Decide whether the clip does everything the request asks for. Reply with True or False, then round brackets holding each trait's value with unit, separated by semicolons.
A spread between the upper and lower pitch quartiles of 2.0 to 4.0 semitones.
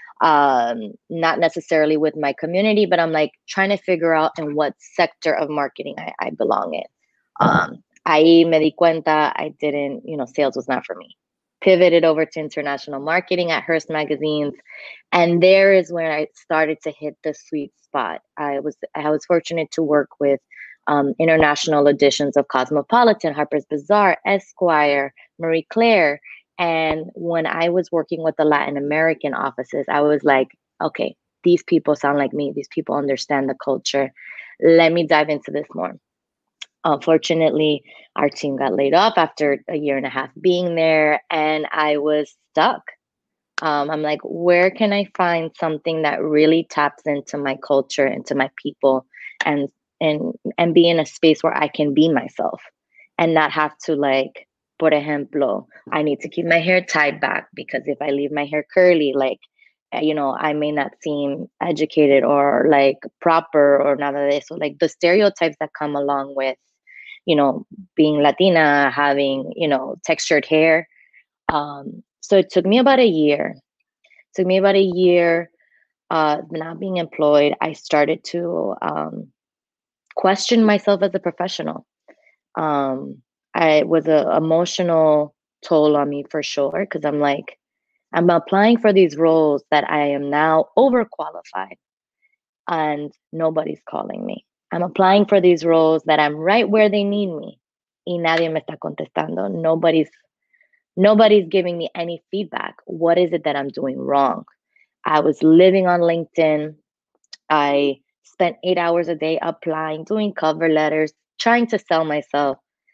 True (3.0 semitones)